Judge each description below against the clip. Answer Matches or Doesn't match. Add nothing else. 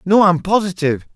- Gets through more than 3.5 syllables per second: Matches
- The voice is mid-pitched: Matches